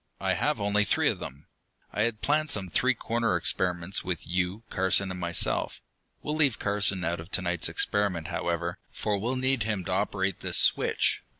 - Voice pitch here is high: No, low, 100 Hz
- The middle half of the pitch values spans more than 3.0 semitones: Yes, average, 3.8 semitones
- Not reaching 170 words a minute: No, average, 185 wpm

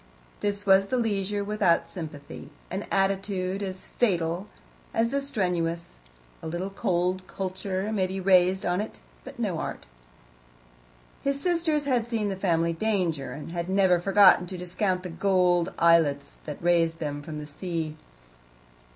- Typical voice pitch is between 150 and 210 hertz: Yes, medium, 185 Hz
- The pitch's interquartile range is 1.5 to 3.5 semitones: Yes, average, 3.0 semitones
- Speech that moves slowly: No, average, 150 wpm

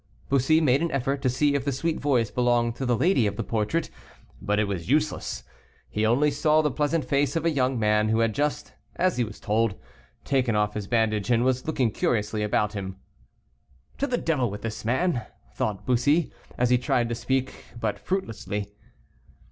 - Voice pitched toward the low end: Yes, low, 125 Hz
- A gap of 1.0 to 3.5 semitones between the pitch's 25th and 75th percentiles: No, average, 5.0 semitones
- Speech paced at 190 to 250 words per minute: Yes, average, 195 wpm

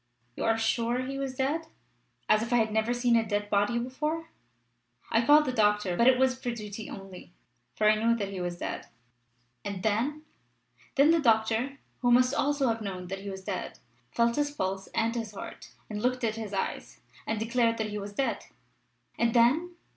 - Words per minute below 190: No, average, 200 wpm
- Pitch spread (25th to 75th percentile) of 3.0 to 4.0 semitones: Yes, average, 3.6 semitones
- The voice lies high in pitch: Yes, high, 230 Hz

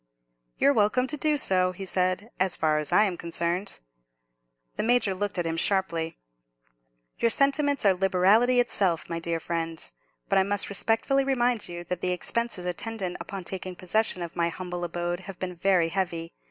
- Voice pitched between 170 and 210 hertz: Yes, medium, 185 Hz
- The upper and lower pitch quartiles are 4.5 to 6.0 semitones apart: No, average, 4.0 semitones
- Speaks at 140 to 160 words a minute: No, average, 175 wpm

